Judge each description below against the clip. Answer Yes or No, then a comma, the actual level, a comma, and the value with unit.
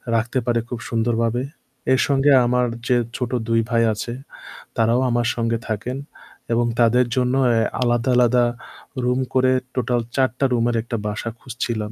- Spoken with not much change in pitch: Yes, narrow, 1.4 semitones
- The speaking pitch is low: Yes, low, 120 Hz